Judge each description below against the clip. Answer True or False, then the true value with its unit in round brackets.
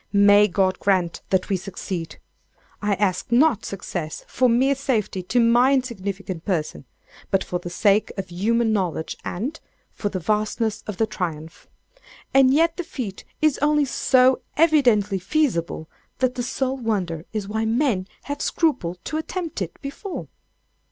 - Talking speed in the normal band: True (150 wpm)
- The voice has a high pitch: True (215 Hz)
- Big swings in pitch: True (5.8 semitones)